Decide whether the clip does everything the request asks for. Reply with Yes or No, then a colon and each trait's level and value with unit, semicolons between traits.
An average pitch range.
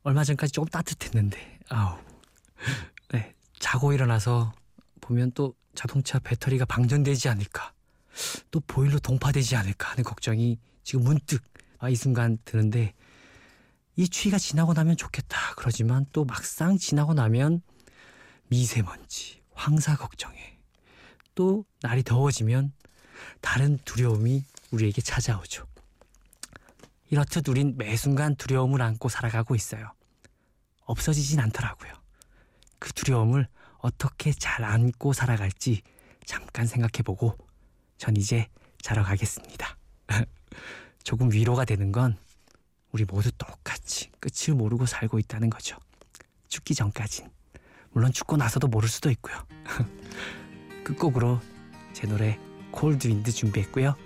Yes: average, 4.2 semitones